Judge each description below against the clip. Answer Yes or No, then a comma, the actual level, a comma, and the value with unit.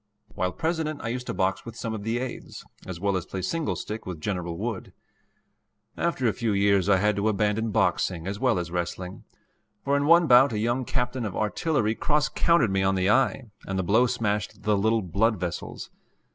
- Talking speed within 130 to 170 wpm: No, fast, 205 wpm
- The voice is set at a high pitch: No, low, 110 Hz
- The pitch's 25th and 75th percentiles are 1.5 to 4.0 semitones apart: No, average, 4.6 semitones